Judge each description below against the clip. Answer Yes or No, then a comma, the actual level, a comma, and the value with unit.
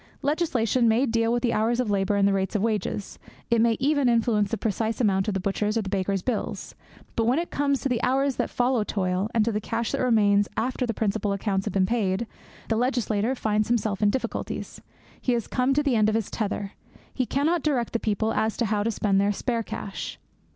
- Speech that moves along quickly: Yes, fast, 230 wpm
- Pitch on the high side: Yes, high, 225 Hz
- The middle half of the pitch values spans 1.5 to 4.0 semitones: Yes, average, 3.1 semitones